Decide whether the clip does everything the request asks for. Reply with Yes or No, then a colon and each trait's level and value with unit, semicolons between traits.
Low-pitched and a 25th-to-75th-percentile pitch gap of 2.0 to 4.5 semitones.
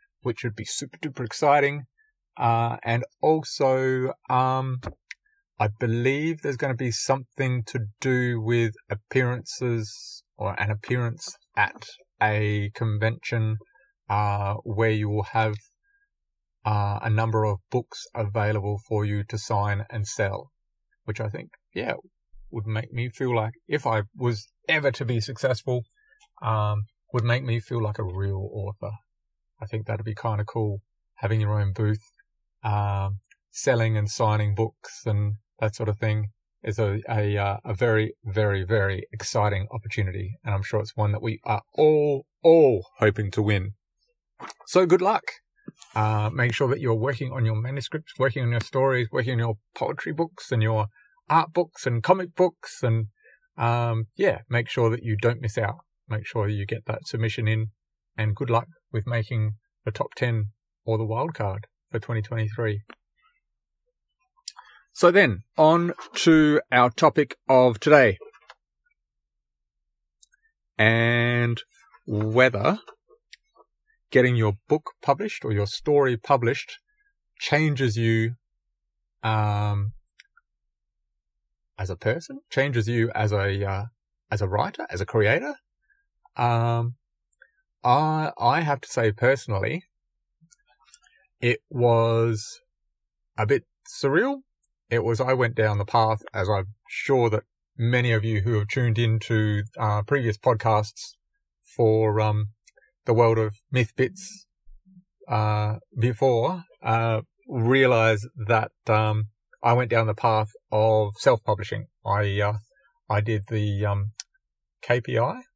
Yes: low, 115 Hz; average, 4.0 semitones